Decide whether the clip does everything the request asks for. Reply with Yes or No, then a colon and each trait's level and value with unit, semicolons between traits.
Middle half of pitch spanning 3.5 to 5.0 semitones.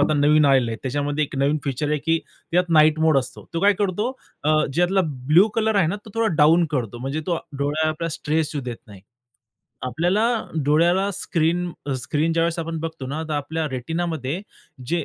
No: average, 3.1 semitones